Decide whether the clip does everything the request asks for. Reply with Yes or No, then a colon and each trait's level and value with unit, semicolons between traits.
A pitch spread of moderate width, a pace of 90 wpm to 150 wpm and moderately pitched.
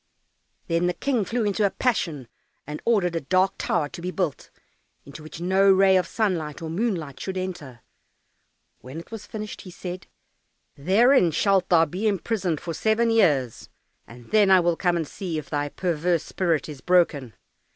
No: average, 4.0 semitones; average, 175 wpm; medium, 180 Hz